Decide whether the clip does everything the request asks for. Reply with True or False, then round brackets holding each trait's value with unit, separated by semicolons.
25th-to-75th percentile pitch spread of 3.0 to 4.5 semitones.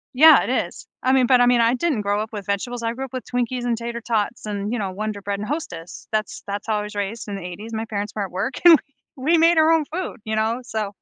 True (3.7 semitones)